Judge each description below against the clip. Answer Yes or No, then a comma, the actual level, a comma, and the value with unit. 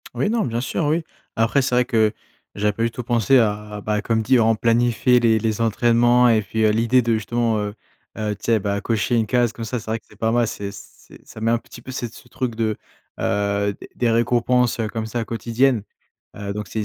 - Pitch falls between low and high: No, low, 115 Hz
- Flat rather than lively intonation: Yes, narrow, 2.0 semitones